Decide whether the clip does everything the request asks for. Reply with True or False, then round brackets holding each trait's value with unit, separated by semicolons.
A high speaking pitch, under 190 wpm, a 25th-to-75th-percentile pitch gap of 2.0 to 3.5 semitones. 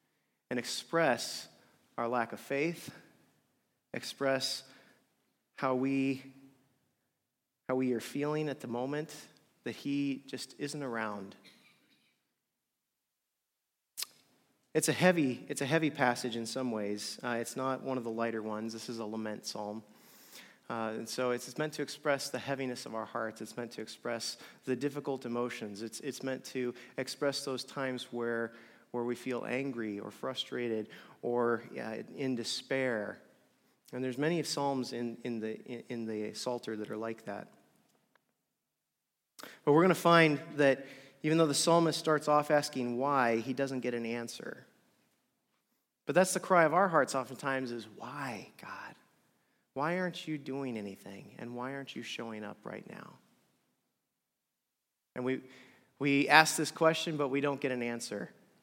False (130 Hz; 155 wpm; 3.1 semitones)